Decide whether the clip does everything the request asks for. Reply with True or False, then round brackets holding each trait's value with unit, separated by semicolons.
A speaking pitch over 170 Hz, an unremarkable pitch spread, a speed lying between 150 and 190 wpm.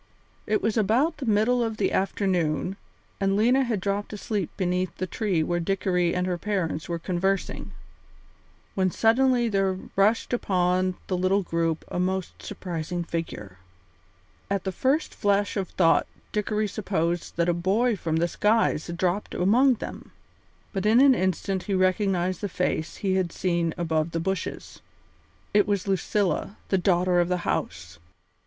True (190 Hz; 3.0 semitones; 160 wpm)